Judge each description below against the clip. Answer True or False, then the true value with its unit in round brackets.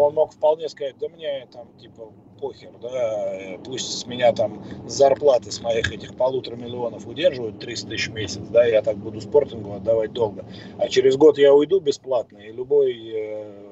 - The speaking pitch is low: True (120 Hz)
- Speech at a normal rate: False (175 wpm)